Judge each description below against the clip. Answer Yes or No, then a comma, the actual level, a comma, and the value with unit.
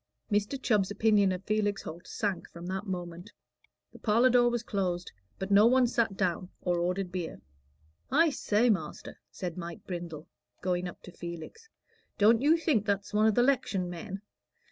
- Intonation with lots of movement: No, average, 4.1 semitones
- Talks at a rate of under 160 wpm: No, average, 170 wpm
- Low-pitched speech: No, high, 200 Hz